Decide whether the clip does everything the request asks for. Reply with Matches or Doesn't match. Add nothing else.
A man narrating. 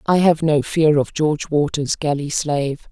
Doesn't match